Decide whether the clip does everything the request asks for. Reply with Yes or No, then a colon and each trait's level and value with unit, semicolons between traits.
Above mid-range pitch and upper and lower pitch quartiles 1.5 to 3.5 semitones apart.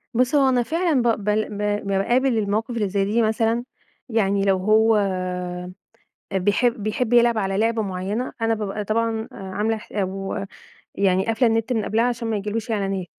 Yes: high, 215 Hz; average, 2.7 semitones